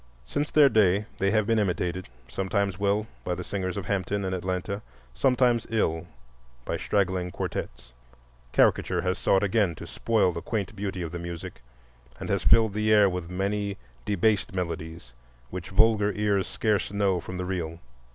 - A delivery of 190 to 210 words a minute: No, average, 160 wpm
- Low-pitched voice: Yes, very low, 95 Hz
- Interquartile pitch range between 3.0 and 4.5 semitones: No, narrow, 2.6 semitones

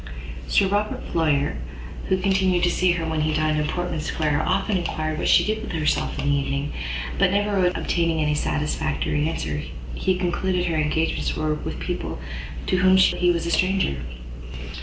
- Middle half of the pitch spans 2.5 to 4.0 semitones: Yes, average, 3.4 semitones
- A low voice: No, medium, 165 Hz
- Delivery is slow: No, average, 175 wpm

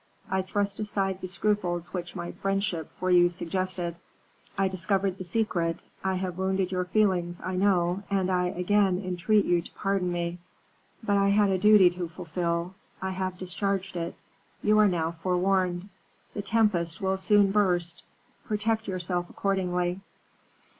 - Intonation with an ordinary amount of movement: No, narrow, 2.0 semitones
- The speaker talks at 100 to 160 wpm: Yes, average, 155 wpm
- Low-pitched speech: No, medium, 185 Hz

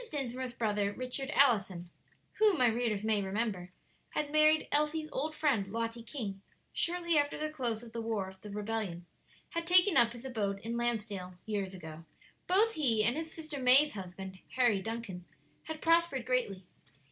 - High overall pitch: Yes, high, 235 Hz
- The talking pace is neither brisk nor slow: Yes, average, 165 wpm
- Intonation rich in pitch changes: Yes, wide, 6.7 semitones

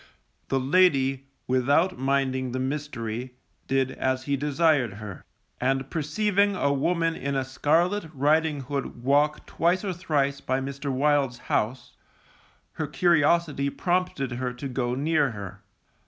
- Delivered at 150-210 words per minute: No, slow, 135 wpm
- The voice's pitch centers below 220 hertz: Yes, medium, 140 Hz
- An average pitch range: Yes, average, 3.4 semitones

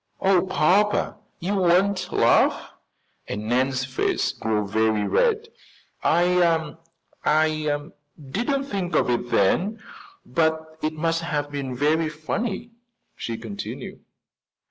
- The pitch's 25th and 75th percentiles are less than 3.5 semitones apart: No, wide, 5.6 semitones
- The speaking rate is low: Yes, slow, 110 wpm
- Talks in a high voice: No, medium, 160 Hz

